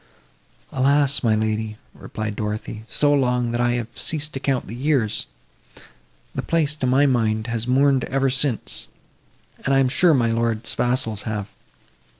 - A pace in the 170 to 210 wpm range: No, average, 155 wpm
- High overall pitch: No, low, 125 Hz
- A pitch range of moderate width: Yes, average, 3.7 semitones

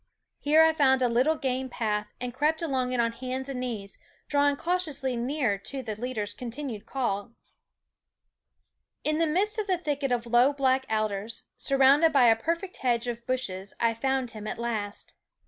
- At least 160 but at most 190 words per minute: Yes, average, 175 wpm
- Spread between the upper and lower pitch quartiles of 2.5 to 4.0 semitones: Yes, average, 3.7 semitones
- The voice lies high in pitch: Yes, very high, 255 Hz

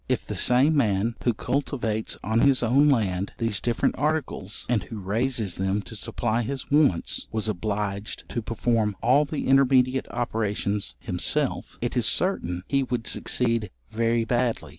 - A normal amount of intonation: Yes, average, 3.5 semitones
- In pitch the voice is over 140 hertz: No, low, 115 Hz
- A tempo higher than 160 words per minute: No, average, 155 wpm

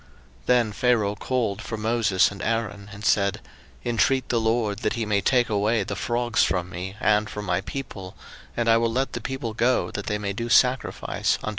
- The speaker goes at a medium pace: No, fast, 210 wpm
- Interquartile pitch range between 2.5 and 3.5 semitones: Yes, average, 2.9 semitones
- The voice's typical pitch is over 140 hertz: No, low, 110 Hz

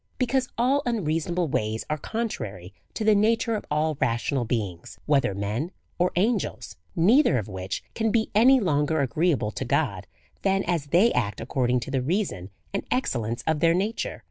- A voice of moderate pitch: Yes, medium, 155 Hz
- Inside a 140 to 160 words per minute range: No, average, 170 wpm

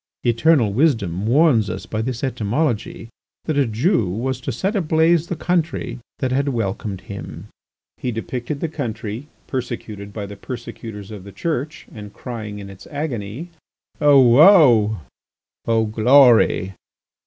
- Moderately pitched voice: No, low, 120 Hz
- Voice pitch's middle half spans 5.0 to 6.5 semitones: Yes, average, 5.3 semitones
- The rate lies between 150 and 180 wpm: No, average, 140 wpm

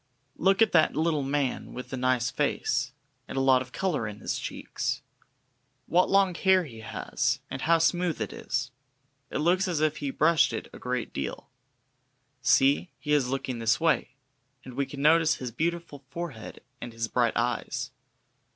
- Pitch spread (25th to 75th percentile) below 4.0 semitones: No, average, 4.9 semitones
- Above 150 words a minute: Yes, average, 175 wpm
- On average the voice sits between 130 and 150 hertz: Yes, medium, 140 Hz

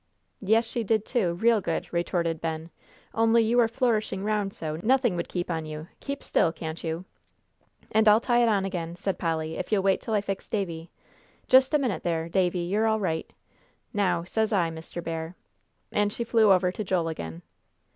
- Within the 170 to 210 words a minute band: Yes, average, 195 wpm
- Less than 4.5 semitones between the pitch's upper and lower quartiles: No, average, 4.8 semitones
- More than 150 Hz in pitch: Yes, high, 190 Hz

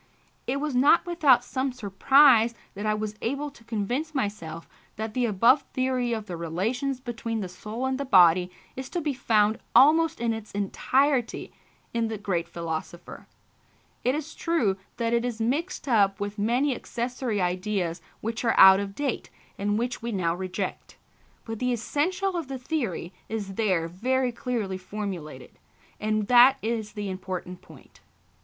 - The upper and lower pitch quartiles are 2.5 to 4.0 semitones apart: No, average, 4.7 semitones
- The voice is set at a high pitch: Yes, high, 225 Hz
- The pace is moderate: Yes, average, 160 wpm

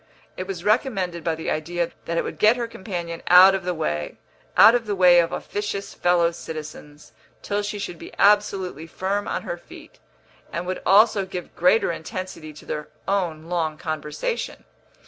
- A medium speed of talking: Yes, average, 175 wpm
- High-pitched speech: No, medium, 180 Hz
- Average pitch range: Yes, average, 3.5 semitones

